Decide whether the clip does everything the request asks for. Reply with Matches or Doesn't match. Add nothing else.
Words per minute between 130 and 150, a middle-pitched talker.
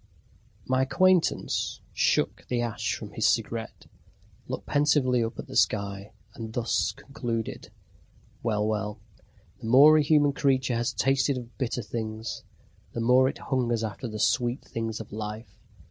Doesn't match